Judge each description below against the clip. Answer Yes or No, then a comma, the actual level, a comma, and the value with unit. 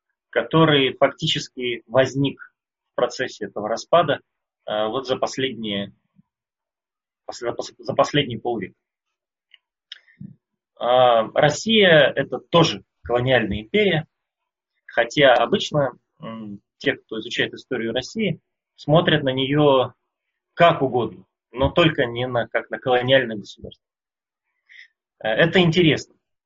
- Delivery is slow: Yes, slow, 90 wpm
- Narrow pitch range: No, average, 4.4 semitones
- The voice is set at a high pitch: No, low, 135 Hz